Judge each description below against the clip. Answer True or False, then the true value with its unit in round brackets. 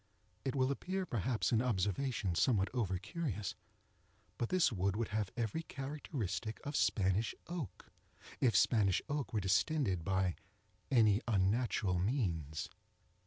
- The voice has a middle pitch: False (110 Hz)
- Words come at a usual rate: False (125 wpm)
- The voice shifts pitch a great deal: True (5.7 semitones)